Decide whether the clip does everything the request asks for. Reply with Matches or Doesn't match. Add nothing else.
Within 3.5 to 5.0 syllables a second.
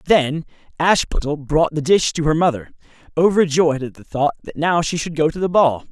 Doesn't match